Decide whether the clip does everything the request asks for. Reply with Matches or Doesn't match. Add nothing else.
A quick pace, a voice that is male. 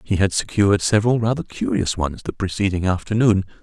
Doesn't match